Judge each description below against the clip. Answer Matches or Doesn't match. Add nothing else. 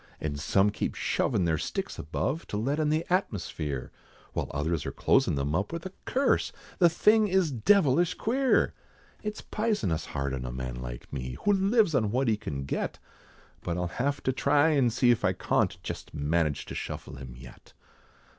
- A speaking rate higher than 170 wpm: Matches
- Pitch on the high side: Doesn't match